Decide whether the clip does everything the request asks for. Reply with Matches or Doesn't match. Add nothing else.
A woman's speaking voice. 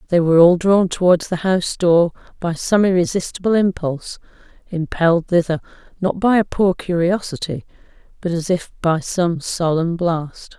Matches